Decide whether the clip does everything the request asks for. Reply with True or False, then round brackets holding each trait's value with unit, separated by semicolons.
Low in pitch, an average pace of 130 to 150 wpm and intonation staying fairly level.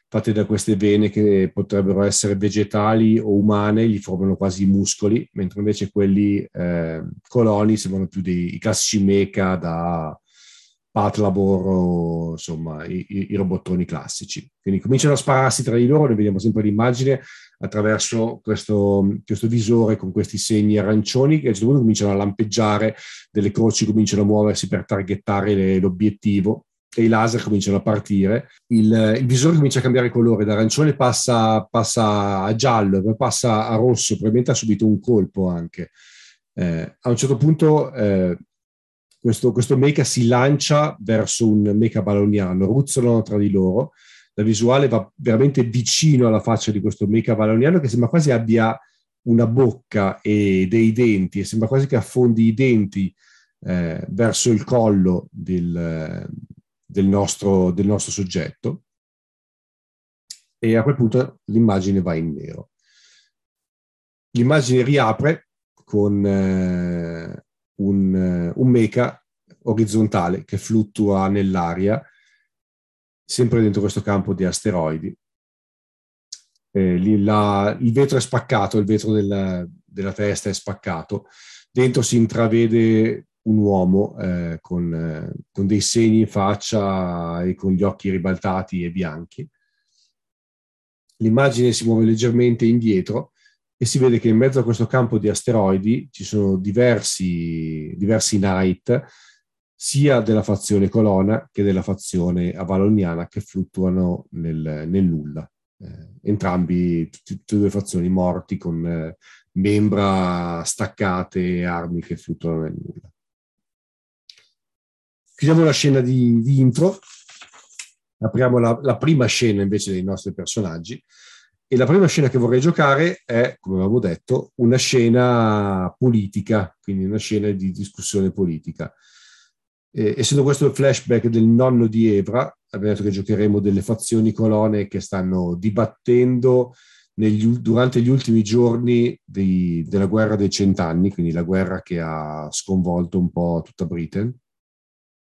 False (105 Hz; 140 wpm; 3.7 semitones)